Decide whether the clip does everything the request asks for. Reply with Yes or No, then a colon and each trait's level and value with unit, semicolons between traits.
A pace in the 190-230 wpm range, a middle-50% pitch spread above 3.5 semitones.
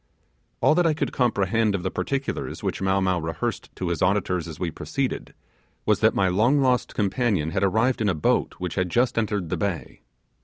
Yes: average, 200 wpm; average, 4.7 semitones